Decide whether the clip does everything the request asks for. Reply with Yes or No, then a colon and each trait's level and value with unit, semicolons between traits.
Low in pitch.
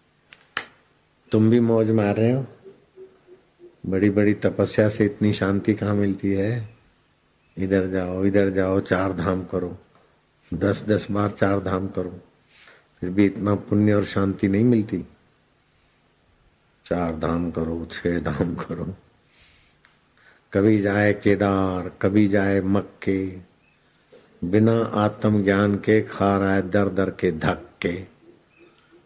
Yes: low, 100 Hz